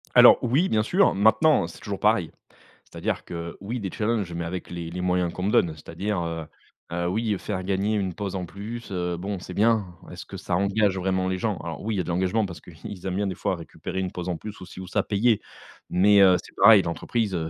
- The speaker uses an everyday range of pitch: Yes, average, 3.0 semitones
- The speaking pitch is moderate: No, very low, 95 Hz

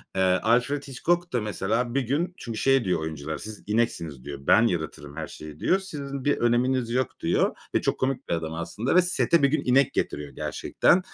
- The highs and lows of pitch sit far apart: Yes, wide, 8.4 semitones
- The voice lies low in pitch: Yes, low, 120 Hz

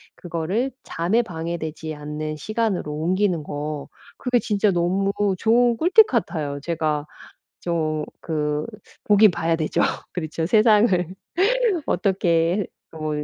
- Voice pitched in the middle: Yes, medium, 170 Hz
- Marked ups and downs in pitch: No, average, 4.9 semitones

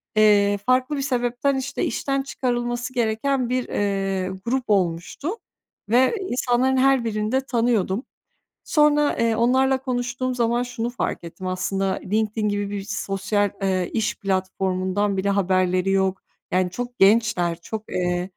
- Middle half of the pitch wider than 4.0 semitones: Yes, average, 4.4 semitones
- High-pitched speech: Yes, high, 220 Hz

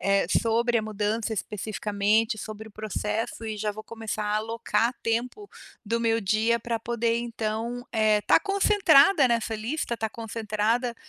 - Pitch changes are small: Yes, narrow, 1.6 semitones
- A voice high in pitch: Yes, high, 225 Hz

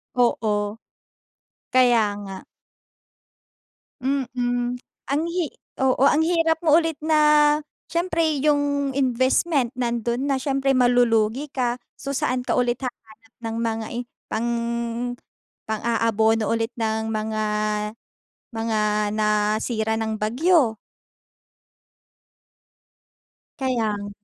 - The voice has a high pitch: Yes, high, 245 Hz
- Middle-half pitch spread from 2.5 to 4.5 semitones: Yes, average, 4.0 semitones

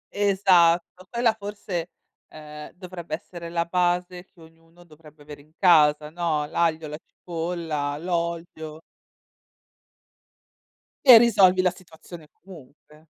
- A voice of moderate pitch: Yes, medium, 170 Hz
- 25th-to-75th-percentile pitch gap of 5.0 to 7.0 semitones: No, average, 2.7 semitones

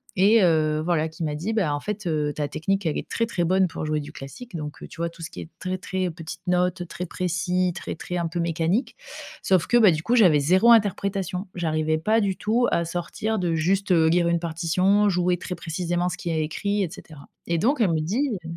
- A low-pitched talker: No, medium, 175 Hz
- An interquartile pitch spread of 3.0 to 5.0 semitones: Yes, average, 3.3 semitones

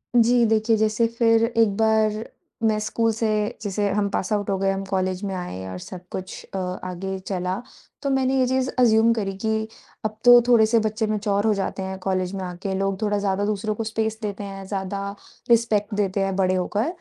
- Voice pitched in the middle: No, high, 210 Hz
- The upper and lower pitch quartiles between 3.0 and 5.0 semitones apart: No, narrow, 2.4 semitones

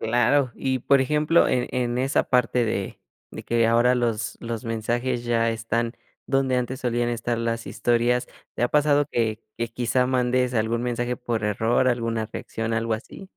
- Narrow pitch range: Yes, narrow, 1.6 semitones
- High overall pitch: No, low, 120 Hz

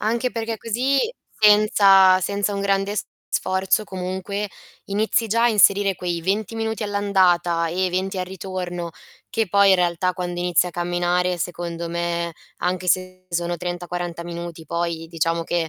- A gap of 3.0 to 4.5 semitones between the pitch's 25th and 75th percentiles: No, narrow, 2.6 semitones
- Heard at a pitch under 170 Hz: No, medium, 185 Hz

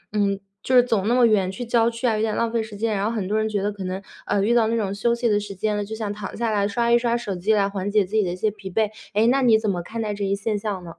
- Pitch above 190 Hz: Yes, high, 210 Hz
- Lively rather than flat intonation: No, narrow, 2.4 semitones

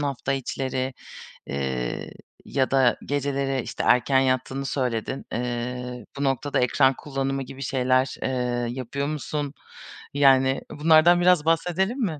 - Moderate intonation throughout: No, narrow, 2.2 semitones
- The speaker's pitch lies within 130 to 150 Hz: Yes, low, 135 Hz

